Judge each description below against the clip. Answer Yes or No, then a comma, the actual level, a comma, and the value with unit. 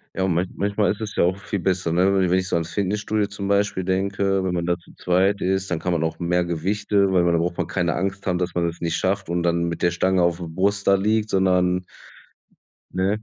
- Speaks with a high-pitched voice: No, very low, 95 Hz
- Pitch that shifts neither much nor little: No, narrow, 2.2 semitones